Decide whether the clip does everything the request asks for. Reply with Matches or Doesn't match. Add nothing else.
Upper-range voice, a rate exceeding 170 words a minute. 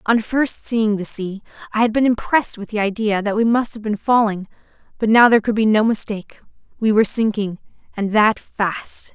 Matches